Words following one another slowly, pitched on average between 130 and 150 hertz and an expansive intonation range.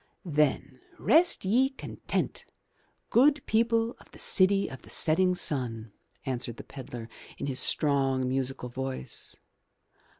Yes: slow, 125 wpm; medium, 140 Hz; wide, 7.7 semitones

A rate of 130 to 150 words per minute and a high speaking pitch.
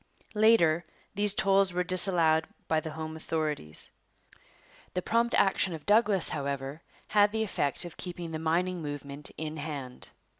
No: average, 145 wpm; medium, 165 Hz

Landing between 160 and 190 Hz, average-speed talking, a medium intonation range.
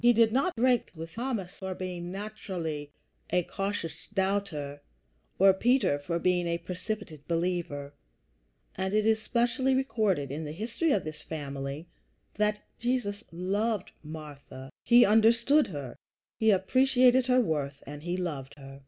No: medium, 185 Hz; average, 145 wpm; wide, 6.3 semitones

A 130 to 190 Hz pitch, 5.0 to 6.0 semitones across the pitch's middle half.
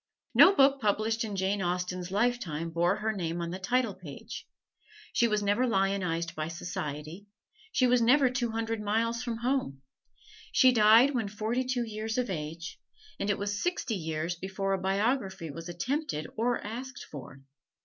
No: high, 205 Hz; wide, 5.4 semitones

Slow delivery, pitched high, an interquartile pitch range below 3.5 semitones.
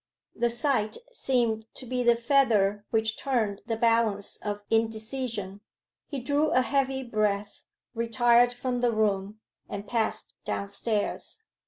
Yes: slow, 130 wpm; high, 230 Hz; average, 2.9 semitones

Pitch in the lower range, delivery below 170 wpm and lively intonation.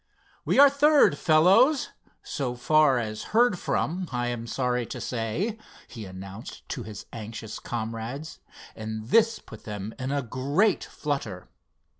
Yes: low, 125 Hz; average, 140 wpm; wide, 7.7 semitones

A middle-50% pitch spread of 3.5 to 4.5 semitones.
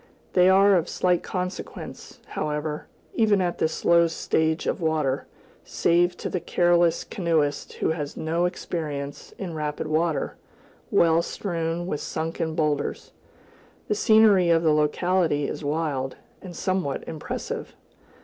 No: average, 2.7 semitones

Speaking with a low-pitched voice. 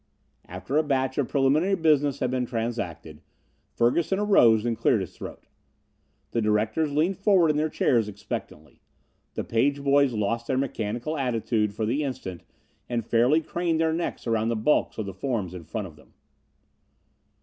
Yes: low, 120 Hz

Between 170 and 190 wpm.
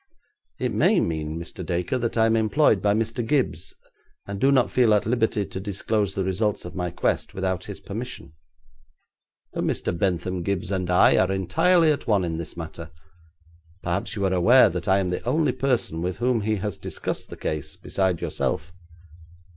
Yes: average, 185 wpm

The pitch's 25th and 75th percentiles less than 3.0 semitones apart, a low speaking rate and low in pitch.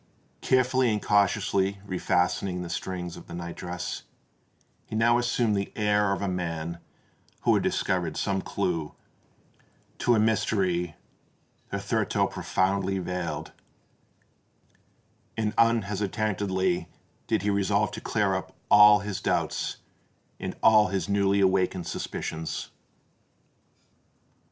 Yes: narrow, 2.6 semitones; slow, 115 wpm; low, 100 Hz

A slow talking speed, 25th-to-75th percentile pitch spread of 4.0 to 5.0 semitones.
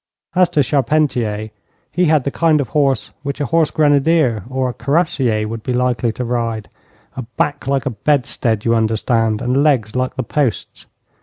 No: average, 175 wpm; average, 4.3 semitones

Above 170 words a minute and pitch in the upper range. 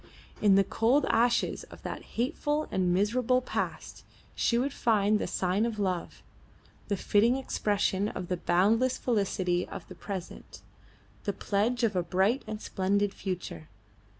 No: average, 150 wpm; high, 205 Hz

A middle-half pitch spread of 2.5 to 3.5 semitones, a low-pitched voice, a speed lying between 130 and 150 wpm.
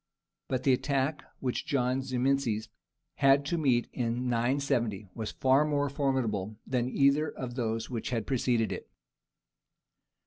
Yes: average, 2.9 semitones; low, 130 Hz; average, 140 wpm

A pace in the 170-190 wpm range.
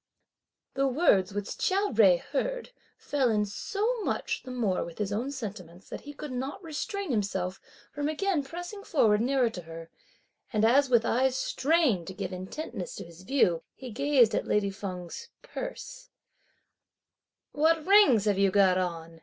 No: average, 160 wpm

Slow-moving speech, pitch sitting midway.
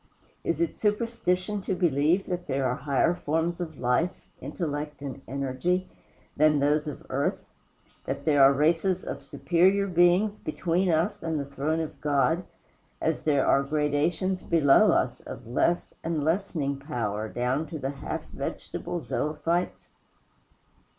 No: average, 145 wpm; medium, 155 Hz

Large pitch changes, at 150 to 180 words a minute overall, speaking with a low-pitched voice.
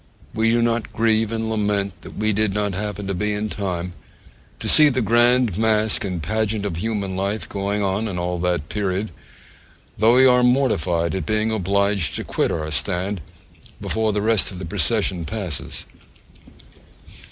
No: average, 2.9 semitones; average, 170 wpm; low, 105 Hz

